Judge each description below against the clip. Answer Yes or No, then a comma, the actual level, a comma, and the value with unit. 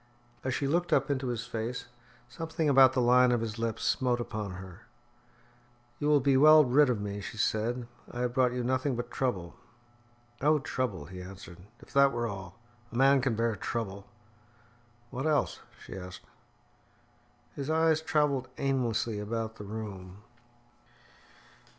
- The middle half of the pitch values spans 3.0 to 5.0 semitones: Yes, average, 4.3 semitones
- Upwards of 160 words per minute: No, average, 155 wpm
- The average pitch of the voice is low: Yes, low, 120 Hz